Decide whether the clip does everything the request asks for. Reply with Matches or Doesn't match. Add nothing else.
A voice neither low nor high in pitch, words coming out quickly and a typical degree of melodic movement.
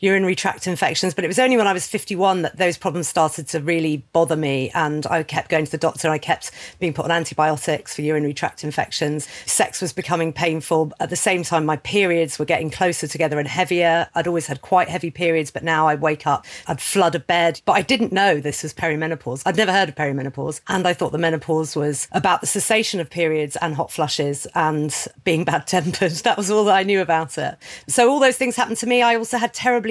Matches